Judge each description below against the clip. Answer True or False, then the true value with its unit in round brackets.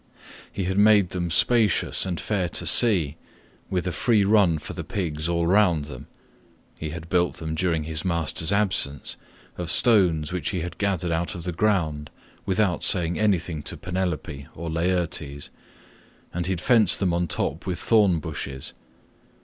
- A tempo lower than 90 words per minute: False (165 wpm)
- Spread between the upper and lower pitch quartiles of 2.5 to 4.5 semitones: True (3.1 semitones)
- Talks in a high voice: False (90 Hz)